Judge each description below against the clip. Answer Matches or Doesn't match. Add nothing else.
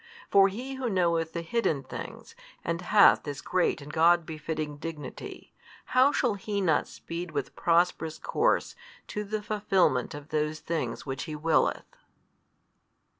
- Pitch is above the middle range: Doesn't match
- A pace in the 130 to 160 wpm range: Matches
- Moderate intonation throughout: Matches